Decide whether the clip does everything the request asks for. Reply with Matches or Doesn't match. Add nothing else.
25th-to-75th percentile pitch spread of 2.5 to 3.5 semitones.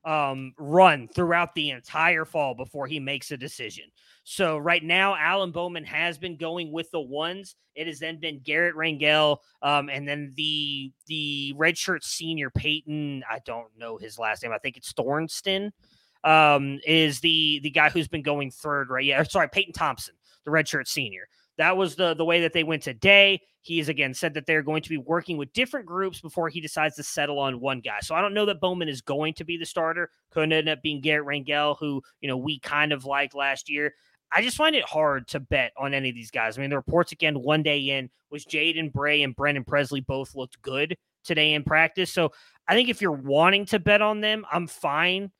Matches